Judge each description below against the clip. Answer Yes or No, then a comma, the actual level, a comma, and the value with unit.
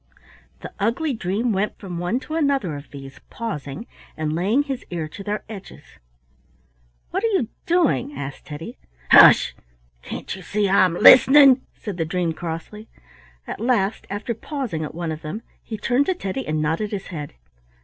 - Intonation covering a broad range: Yes, wide, 7.1 semitones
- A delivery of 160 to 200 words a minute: Yes, average, 170 wpm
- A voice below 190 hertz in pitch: No, high, 200 Hz